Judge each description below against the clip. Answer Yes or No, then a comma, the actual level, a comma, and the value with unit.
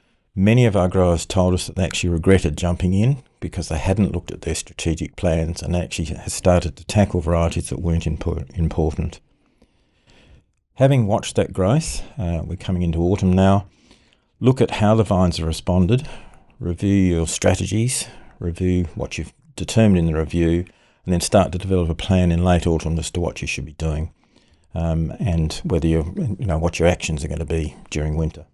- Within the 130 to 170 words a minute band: No, average, 185 wpm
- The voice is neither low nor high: No, very low, 90 Hz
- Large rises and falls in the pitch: No, average, 2.7 semitones